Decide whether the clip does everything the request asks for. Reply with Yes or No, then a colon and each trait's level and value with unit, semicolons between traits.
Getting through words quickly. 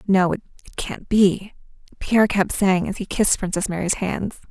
No: average, 175 wpm